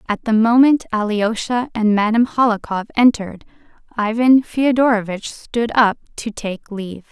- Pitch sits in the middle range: No, high, 225 Hz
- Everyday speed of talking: No, slow, 125 wpm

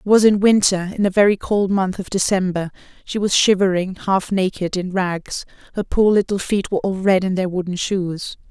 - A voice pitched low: No, high, 190 Hz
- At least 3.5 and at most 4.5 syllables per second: No, 5.1 syllables/s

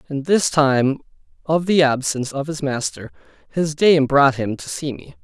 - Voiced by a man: Yes, male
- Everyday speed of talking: Yes, average, 185 wpm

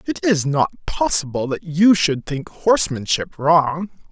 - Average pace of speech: Yes, average, 145 wpm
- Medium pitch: Yes, medium, 165 Hz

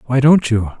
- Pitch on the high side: No, low, 125 Hz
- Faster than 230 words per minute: No, fast, 225 wpm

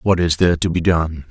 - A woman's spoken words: No, male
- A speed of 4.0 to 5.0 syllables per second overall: No, 5.7 syllables/s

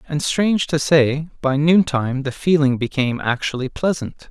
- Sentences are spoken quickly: No, average, 155 wpm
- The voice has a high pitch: No, medium, 145 Hz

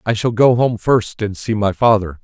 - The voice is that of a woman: No, male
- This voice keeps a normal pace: No, fast, 240 wpm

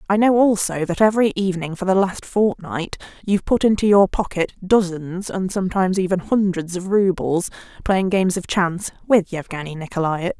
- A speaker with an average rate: Yes, average, 165 wpm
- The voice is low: No, medium, 185 Hz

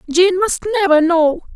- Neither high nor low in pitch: No, very high, 350 Hz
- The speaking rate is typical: Yes, average, 155 wpm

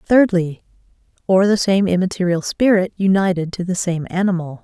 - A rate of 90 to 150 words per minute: Yes, average, 140 wpm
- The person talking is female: Yes, female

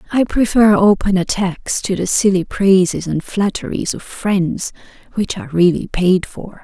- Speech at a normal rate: Yes, average, 155 wpm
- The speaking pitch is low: No, high, 190 Hz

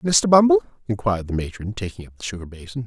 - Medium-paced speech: No, fast, 210 wpm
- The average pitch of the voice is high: No, low, 105 Hz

